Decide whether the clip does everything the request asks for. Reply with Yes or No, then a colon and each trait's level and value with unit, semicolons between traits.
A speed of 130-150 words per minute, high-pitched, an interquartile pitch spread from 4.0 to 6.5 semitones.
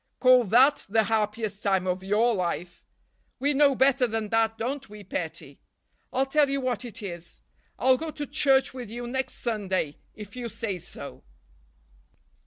No: average, 165 wpm; high, 230 Hz; average, 4.3 semitones